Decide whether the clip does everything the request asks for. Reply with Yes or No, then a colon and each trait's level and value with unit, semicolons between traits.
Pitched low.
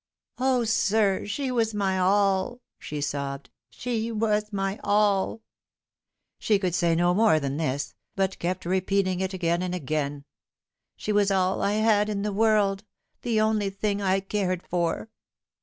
No: high, 195 Hz